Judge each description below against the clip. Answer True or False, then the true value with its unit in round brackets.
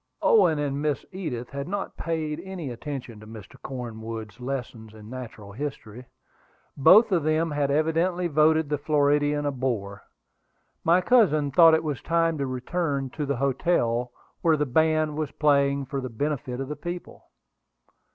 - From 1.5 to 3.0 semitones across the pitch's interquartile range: False (4.0 semitones)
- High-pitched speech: False (145 Hz)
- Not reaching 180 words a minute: True (160 wpm)